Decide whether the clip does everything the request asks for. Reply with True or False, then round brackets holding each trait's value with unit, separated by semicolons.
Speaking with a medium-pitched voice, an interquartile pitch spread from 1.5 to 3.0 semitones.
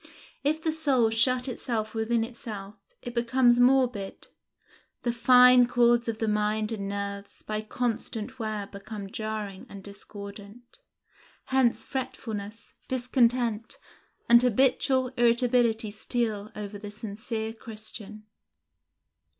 False (225 Hz; 2.7 semitones)